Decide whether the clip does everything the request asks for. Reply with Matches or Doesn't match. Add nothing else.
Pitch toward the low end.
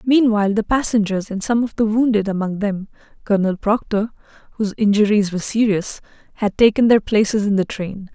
Doesn't match